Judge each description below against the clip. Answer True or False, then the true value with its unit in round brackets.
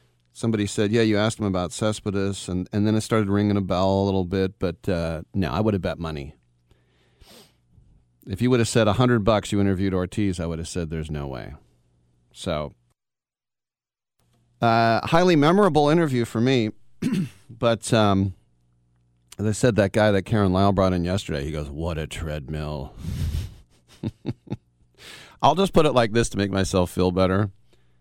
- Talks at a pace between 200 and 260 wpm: False (170 wpm)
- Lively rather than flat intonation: True (5.9 semitones)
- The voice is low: True (95 Hz)